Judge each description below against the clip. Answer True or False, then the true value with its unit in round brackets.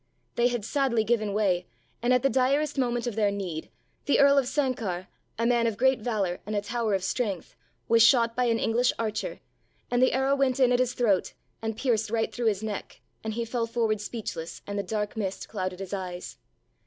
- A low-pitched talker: False (230 Hz)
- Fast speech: True (210 wpm)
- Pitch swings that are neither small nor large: True (3.3 semitones)